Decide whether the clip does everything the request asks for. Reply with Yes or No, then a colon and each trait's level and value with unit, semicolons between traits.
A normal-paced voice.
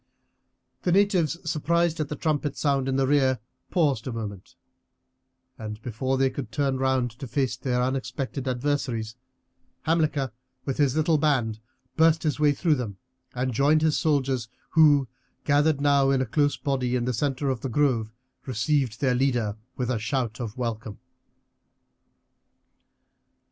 Yes: average, 150 wpm